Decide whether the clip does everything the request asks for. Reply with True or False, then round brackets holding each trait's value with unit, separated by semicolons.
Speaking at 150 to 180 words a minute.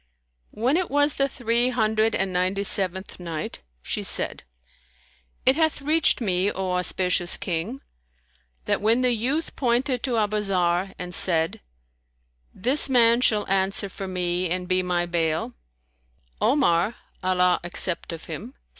False (140 wpm)